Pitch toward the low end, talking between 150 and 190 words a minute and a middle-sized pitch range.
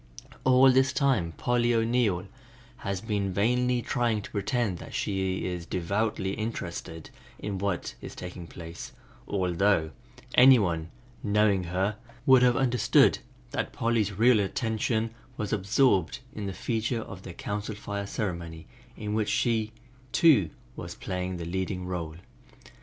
No: low, 105 Hz; slow, 135 wpm; average, 4.0 semitones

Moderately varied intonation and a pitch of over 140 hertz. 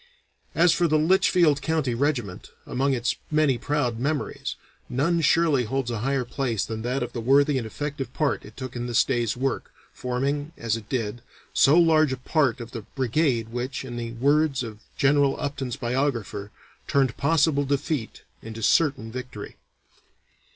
No: average, 3.7 semitones; low, 135 Hz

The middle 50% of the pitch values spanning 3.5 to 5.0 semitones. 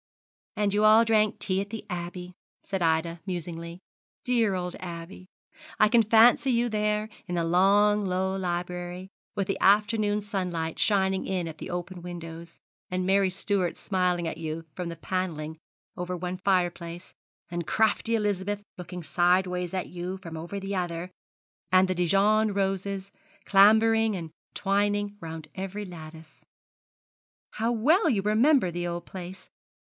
No: average, 2.8 semitones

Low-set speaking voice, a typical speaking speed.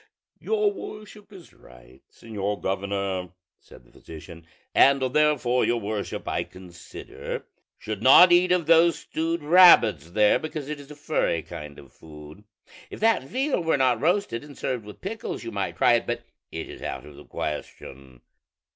Yes: low, 125 Hz; average, 165 wpm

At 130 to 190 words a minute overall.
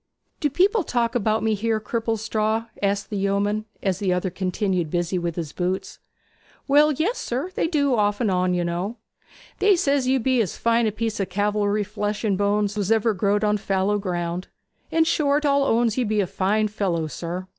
No: average, 200 wpm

